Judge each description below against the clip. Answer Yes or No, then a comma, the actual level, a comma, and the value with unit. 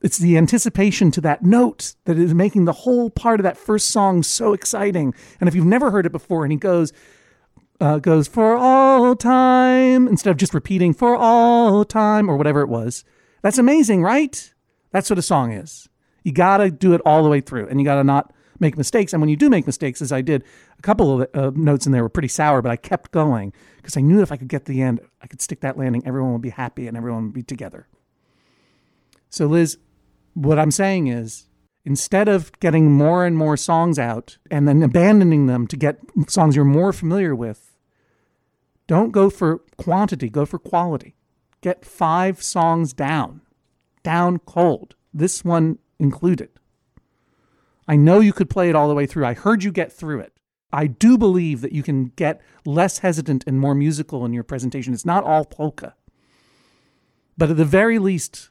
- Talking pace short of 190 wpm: No, average, 200 wpm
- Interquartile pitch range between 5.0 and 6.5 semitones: Yes, average, 5.3 semitones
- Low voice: No, medium, 160 Hz